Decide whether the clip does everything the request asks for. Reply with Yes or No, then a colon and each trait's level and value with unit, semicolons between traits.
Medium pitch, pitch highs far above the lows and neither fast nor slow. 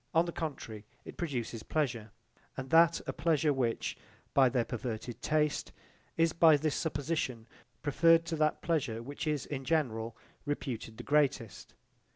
No: medium, 145 Hz; average, 4.9 semitones; average, 150 wpm